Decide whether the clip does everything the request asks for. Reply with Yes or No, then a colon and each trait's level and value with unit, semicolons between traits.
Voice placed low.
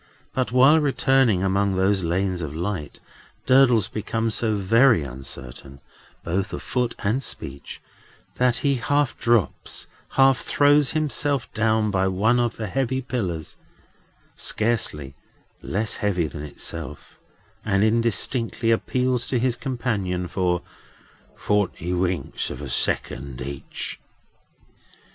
Yes: low, 110 Hz